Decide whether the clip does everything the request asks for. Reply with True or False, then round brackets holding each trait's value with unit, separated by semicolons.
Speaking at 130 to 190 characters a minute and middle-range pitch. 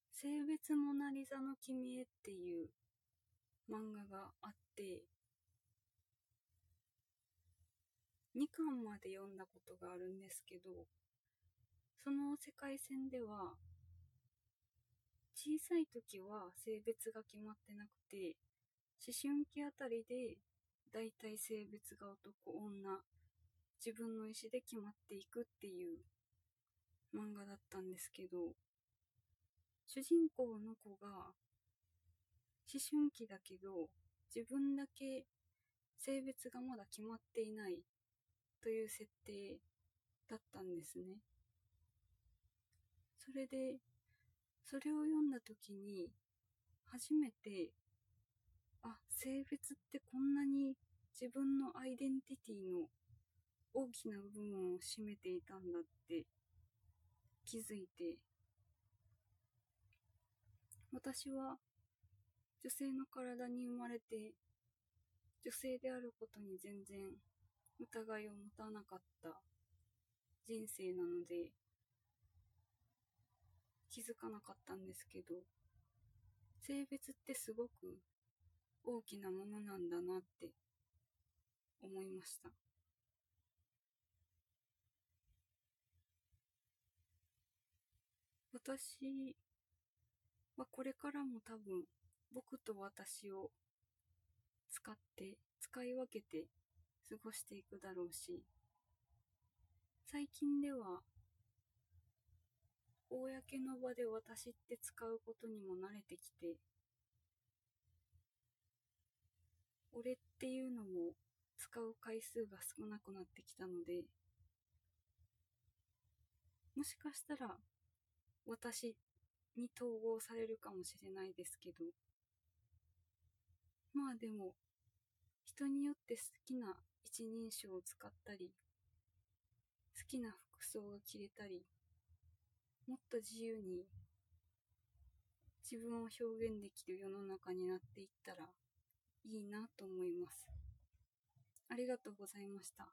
True (185 characters per minute; 175 Hz)